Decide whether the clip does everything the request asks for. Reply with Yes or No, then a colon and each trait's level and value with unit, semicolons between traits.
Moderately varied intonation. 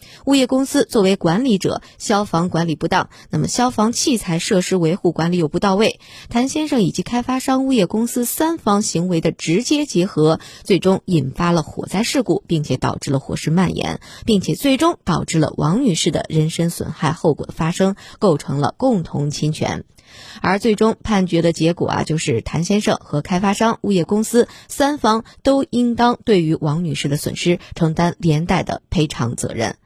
No: wide, 5.7 semitones